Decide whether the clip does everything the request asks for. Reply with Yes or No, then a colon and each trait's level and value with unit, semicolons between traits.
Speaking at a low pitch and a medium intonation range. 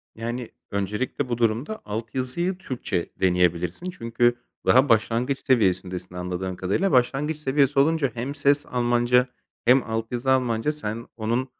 Yes: low, 120 Hz; average, 3.8 semitones